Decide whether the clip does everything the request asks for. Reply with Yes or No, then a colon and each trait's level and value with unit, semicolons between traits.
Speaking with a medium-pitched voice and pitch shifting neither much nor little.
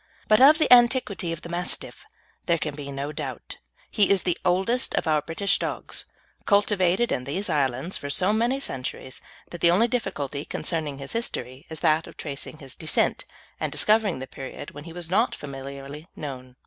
No: medium, 165 Hz; wide, 6.2 semitones